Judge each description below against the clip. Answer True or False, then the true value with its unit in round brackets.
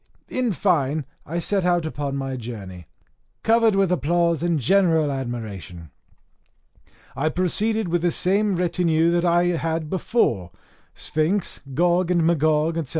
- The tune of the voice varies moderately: True (4.0 semitones)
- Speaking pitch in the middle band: True (165 Hz)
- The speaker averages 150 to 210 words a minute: False (135 wpm)